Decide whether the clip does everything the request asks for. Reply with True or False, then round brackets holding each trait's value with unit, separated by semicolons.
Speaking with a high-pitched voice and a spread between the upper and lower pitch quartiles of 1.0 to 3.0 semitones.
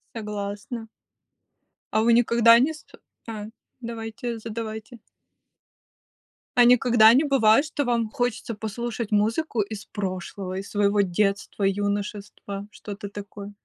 True (220 Hz; 2.5 semitones)